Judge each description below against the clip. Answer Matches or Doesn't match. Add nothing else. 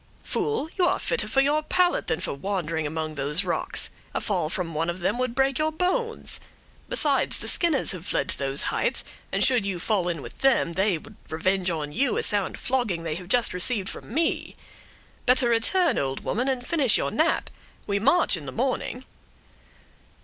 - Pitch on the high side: Matches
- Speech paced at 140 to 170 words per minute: Doesn't match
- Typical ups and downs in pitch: Doesn't match